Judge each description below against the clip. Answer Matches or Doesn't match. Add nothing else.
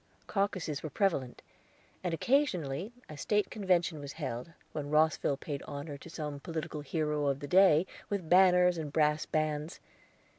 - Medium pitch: Matches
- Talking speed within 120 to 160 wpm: Matches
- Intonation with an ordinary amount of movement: Matches